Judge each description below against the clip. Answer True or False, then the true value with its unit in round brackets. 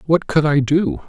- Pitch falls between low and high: True (150 Hz)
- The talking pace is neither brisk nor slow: False (220 wpm)